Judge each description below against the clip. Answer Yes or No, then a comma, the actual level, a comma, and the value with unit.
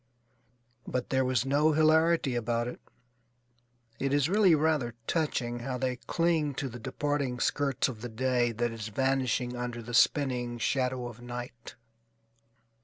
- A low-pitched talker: Yes, low, 125 Hz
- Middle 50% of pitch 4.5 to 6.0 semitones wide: No, average, 3.1 semitones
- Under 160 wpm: Yes, average, 145 wpm